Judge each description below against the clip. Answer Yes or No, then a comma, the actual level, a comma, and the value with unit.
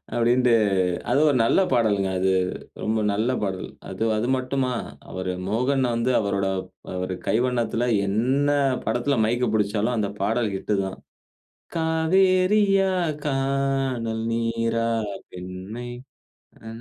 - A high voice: No, low, 115 Hz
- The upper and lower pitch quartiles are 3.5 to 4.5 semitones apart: Yes, average, 4.0 semitones